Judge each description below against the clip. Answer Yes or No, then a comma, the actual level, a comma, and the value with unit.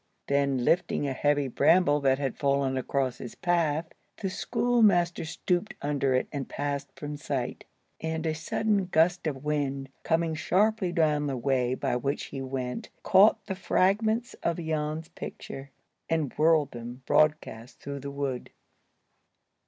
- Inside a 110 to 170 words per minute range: Yes, average, 145 wpm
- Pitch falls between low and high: Yes, medium, 150 Hz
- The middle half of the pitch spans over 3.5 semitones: Yes, average, 3.9 semitones